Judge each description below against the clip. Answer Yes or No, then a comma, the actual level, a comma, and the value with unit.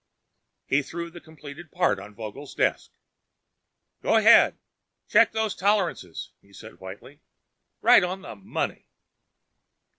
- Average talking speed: No, slow, 120 wpm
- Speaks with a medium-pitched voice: Yes, medium, 145 Hz